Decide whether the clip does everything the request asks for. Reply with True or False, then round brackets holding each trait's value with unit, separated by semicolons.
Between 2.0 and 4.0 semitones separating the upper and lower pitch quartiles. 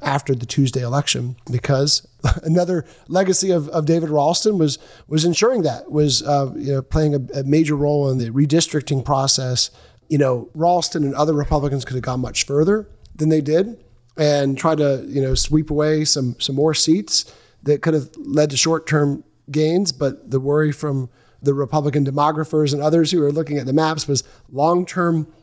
True (2.5 semitones)